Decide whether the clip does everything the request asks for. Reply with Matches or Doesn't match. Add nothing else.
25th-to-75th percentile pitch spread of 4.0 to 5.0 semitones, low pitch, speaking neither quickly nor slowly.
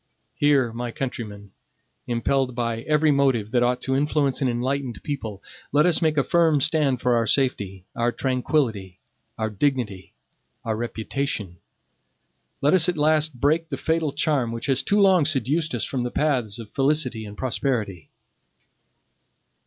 Matches